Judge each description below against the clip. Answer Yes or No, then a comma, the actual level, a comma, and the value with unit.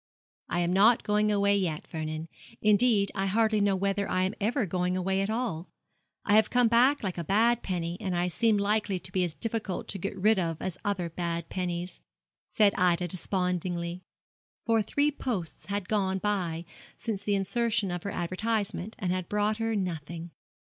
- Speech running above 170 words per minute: Yes, average, 180 wpm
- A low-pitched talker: No, high, 195 Hz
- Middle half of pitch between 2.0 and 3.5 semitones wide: Yes, average, 3.2 semitones